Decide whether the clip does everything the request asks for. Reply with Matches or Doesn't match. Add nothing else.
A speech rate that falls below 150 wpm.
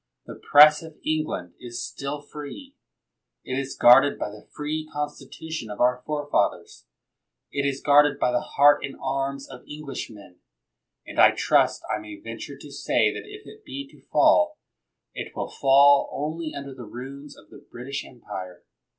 Doesn't match